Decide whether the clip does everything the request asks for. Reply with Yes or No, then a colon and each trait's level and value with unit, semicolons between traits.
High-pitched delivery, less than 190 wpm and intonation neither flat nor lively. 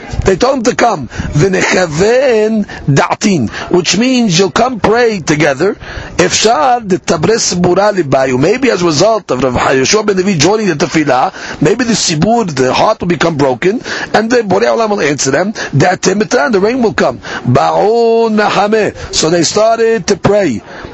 Yes: high, 200 Hz; average, 160 wpm; average, 4.6 semitones